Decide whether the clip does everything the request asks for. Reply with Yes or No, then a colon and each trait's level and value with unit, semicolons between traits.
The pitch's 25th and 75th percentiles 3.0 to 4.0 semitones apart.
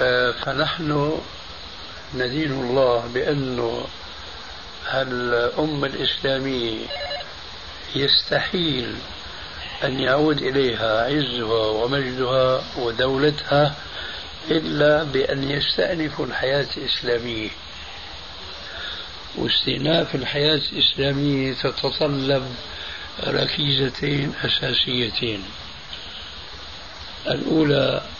No: average, 4.8 semitones